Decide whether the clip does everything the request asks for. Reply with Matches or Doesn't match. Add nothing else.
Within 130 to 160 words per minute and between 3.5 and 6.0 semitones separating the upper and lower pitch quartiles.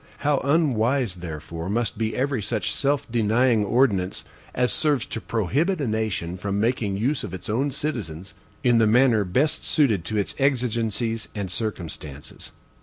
Matches